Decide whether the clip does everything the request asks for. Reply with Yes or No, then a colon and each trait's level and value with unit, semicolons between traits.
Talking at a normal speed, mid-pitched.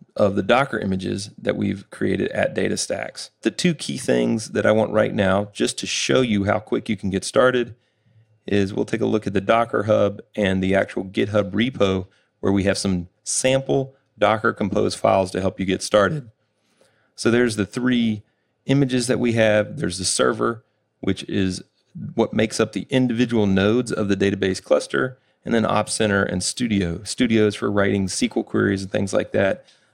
No: average, 185 wpm; low, 105 Hz